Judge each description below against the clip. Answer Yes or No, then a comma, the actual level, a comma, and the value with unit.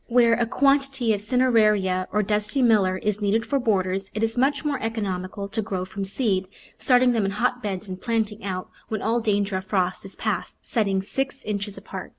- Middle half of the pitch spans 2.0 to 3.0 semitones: No, average, 3.5 semitones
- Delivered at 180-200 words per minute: Yes, average, 195 wpm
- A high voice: Yes, high, 210 Hz